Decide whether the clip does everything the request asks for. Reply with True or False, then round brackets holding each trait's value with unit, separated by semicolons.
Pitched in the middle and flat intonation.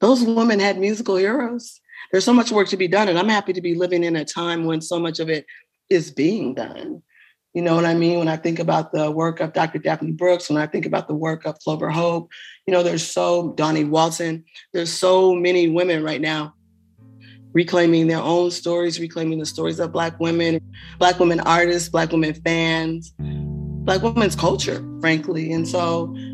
True (165 Hz; 2.0 semitones)